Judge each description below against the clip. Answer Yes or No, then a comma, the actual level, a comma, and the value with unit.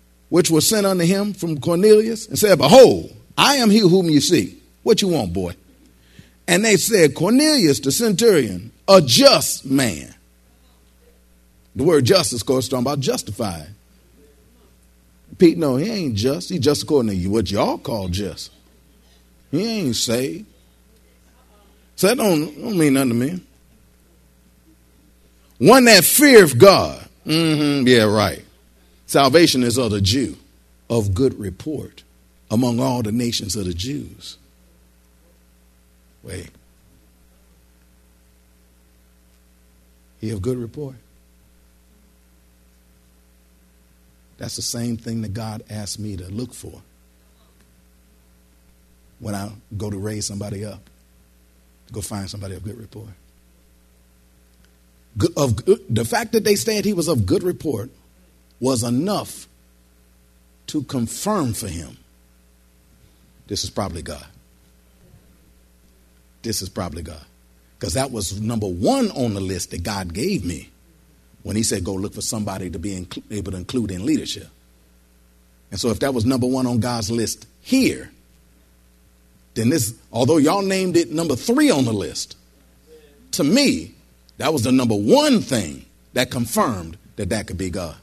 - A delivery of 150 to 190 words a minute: No, average, 140 wpm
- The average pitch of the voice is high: No, very low, 90 Hz